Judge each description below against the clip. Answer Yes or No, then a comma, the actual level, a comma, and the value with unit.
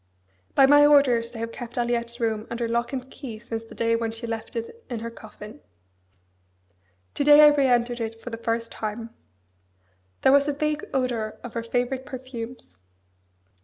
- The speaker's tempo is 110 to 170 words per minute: No, average, 180 wpm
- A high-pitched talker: Yes, high, 235 Hz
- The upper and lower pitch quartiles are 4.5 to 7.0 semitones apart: No, narrow, 2.5 semitones